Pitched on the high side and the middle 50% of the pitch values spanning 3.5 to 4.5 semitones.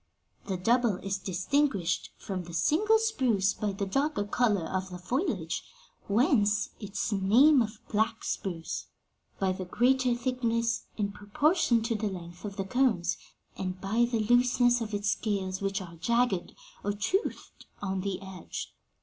Yes: high, 210 Hz; average, 4.2 semitones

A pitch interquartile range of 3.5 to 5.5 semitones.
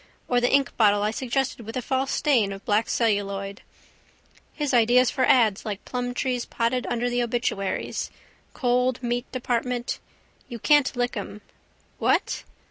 No: average, 2.7 semitones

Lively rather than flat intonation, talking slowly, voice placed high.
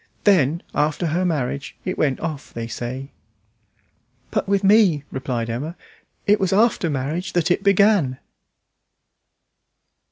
No: wide, 6.1 semitones; slow, 125 wpm; medium, 160 Hz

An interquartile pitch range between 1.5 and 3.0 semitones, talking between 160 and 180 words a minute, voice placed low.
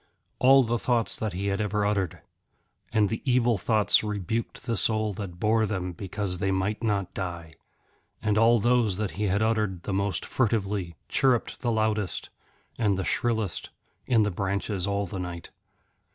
Yes: average, 2.7 semitones; average, 165 wpm; low, 105 Hz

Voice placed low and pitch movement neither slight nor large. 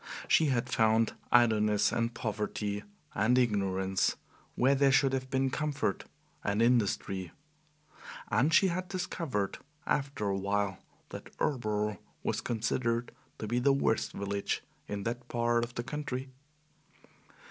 Yes: low, 115 Hz; average, 4.2 semitones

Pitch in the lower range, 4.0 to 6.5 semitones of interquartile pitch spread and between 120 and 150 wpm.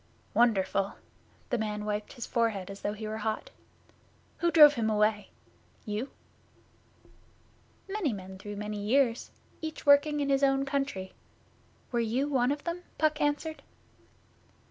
No: high, 235 Hz; wide, 5.5 semitones; average, 140 wpm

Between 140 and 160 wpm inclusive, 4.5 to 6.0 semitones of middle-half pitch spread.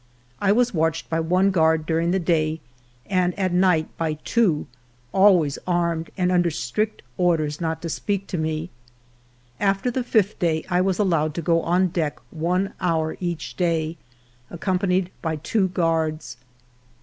No: average, 155 wpm; average, 2.7 semitones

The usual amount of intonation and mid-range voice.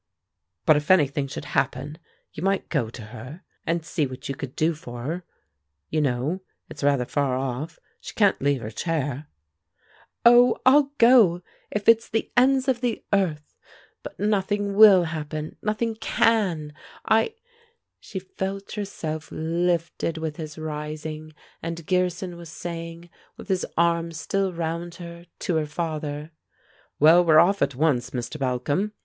Yes: average, 4.4 semitones; medium, 165 Hz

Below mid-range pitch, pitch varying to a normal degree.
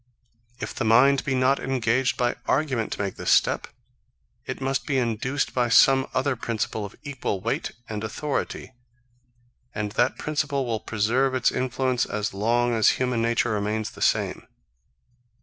Yes: low, 120 Hz; average, 3.1 semitones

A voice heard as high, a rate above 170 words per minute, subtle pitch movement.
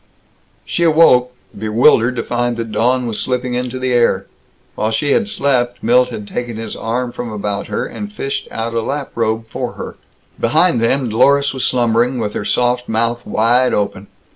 No: low, 120 Hz; average, 180 wpm; narrow, 2.1 semitones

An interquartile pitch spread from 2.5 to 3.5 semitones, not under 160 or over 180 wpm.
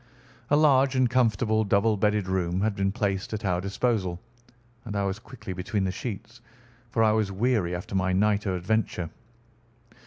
Yes: average, 3.0 semitones; average, 175 wpm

